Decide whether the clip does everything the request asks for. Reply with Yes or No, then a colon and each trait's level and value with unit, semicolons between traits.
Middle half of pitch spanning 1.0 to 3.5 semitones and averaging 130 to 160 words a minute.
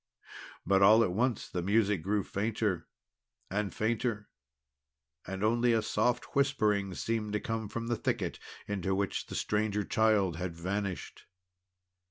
Yes: narrow, 2.6 semitones; average, 140 wpm